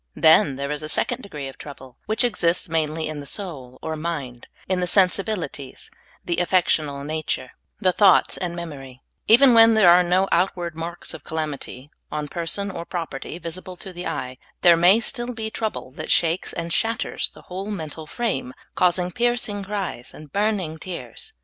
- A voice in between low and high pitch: Yes, medium, 170 Hz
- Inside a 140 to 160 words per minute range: No, average, 175 wpm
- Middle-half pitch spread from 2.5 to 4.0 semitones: No, average, 4.4 semitones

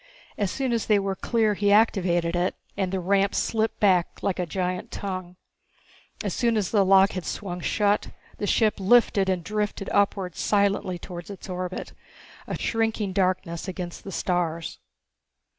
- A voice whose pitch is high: Yes, high, 195 Hz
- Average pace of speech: Yes, average, 160 wpm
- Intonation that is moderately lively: No, narrow, 2.3 semitones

